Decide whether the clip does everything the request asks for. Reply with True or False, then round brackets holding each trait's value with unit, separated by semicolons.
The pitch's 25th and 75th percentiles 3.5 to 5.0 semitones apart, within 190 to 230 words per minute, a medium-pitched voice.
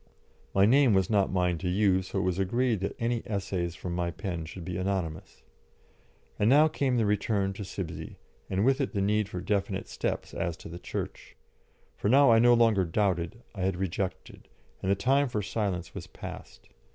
False (3.8 semitones; 195 wpm; 100 Hz)